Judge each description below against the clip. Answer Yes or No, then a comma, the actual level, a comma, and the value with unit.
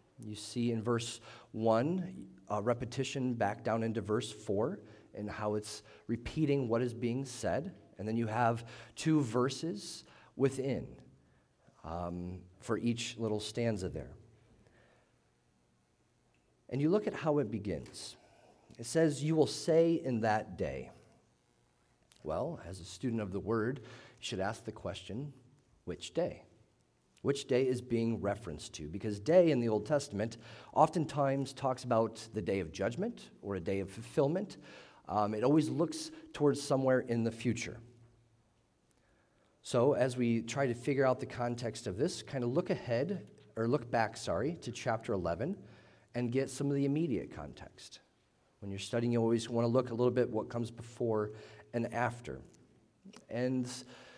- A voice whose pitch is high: No, low, 120 Hz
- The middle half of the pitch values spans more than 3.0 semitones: Yes, average, 3.4 semitones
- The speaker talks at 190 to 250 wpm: No, average, 155 wpm